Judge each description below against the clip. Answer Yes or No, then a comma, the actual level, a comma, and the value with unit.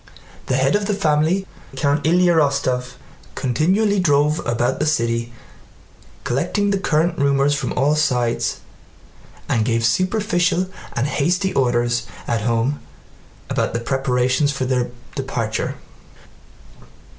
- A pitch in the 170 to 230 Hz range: No, medium, 140 Hz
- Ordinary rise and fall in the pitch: No, wide, 5.7 semitones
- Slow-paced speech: Yes, slow, 120 wpm